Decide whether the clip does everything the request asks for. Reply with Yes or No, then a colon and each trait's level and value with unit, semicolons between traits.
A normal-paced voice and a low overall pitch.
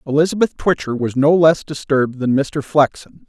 No: average, 165 wpm; medium, 145 Hz